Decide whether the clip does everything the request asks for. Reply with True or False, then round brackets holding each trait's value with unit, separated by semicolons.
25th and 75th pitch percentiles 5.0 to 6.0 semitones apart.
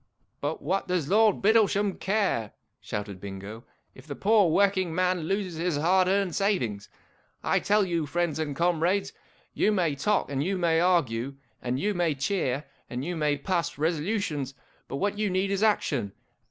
True (5.5 semitones)